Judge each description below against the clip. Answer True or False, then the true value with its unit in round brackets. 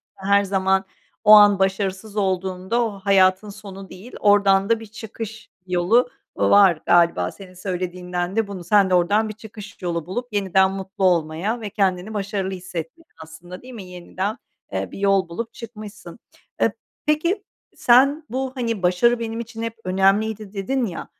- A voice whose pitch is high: True (195 Hz)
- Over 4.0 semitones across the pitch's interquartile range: False (2.9 semitones)